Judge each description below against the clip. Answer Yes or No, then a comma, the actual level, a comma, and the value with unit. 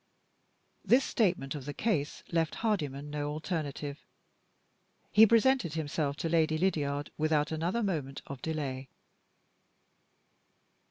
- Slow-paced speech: Yes, slow, 110 wpm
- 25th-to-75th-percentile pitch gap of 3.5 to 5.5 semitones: Yes, average, 3.8 semitones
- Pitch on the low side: No, medium, 155 Hz